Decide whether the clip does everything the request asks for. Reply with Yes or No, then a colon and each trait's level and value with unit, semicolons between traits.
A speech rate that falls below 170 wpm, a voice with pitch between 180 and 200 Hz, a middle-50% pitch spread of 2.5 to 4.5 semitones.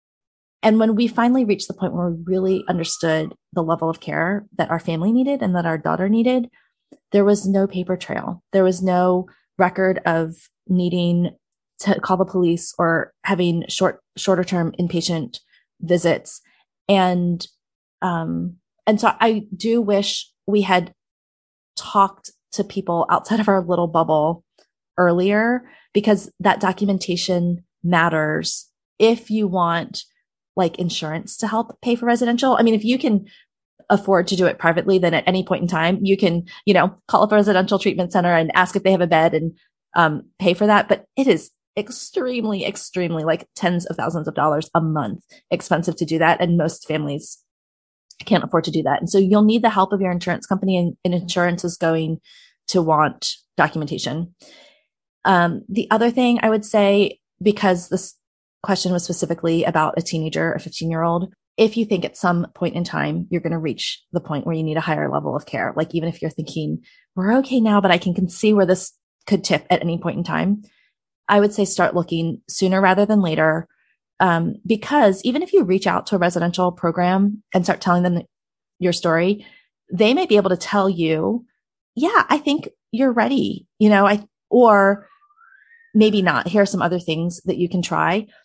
No: average, 185 wpm; medium, 185 Hz; average, 3.4 semitones